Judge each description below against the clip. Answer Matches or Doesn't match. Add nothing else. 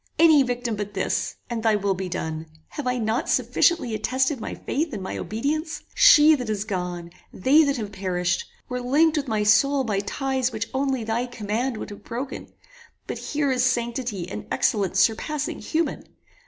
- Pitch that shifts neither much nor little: Matches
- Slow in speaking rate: Doesn't match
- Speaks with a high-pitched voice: Matches